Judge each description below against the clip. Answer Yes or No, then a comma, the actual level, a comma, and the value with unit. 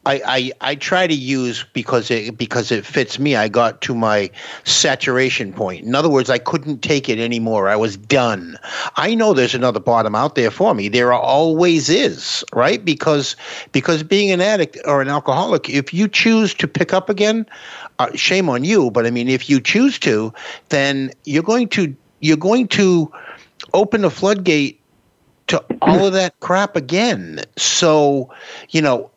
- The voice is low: No, medium, 145 Hz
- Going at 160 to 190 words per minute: Yes, average, 180 wpm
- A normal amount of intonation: No, wide, 7.0 semitones